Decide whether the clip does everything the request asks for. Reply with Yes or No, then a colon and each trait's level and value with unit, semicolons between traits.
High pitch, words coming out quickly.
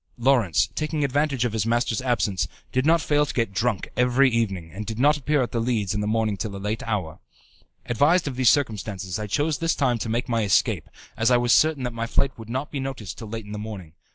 No: low, 115 Hz; fast, 240 wpm